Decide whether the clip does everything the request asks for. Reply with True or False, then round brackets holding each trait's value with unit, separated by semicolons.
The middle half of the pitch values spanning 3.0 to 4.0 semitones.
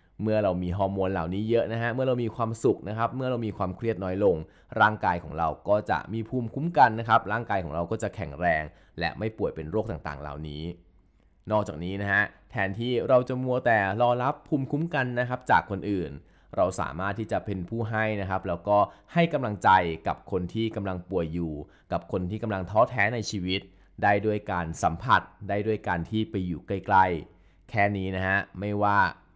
True (3.5 semitones)